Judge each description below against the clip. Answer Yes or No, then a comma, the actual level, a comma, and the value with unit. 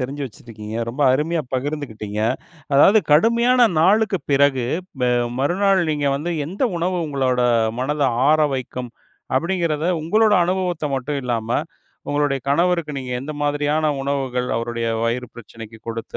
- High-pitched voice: No, medium, 145 Hz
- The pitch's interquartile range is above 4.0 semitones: Yes, average, 5.2 semitones